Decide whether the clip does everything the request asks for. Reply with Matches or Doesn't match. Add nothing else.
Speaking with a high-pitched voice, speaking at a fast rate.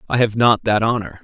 Doesn't match